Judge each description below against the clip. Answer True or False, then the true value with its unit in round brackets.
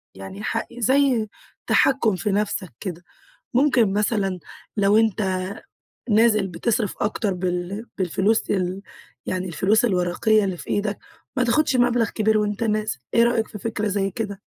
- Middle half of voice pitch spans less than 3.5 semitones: True (2.9 semitones)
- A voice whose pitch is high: True (210 Hz)